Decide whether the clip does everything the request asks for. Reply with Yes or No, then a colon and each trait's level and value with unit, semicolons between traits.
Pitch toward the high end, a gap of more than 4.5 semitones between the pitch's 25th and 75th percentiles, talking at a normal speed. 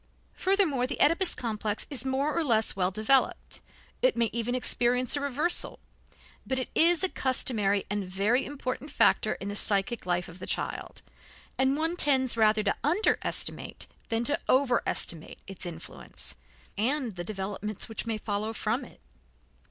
Yes: high, 240 Hz; average, 5.2 semitones; average, 155 wpm